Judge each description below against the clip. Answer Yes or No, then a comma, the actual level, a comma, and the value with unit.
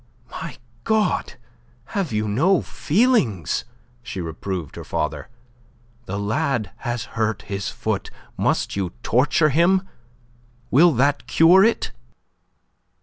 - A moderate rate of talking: No, slow, 110 wpm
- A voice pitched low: Yes, low, 125 Hz